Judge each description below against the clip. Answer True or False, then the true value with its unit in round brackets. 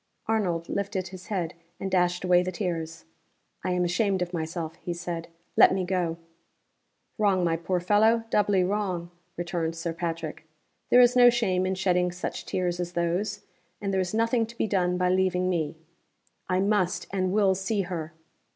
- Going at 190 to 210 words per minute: False (175 wpm)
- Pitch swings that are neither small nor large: False (2.2 semitones)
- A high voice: False (180 Hz)